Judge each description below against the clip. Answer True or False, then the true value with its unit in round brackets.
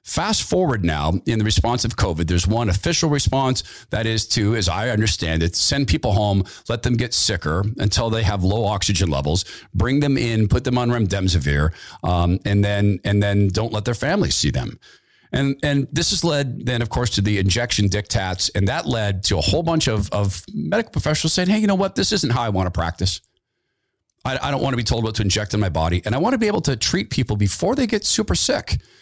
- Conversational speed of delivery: False (230 wpm)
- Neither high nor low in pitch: False (110 Hz)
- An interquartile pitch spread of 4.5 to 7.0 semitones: True (5.3 semitones)